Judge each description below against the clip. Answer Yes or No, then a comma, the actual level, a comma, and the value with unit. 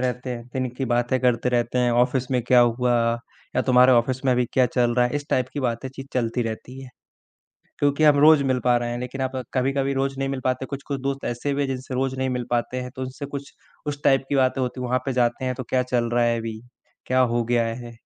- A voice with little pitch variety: Yes, narrow, 1.7 semitones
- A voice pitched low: Yes, low, 130 Hz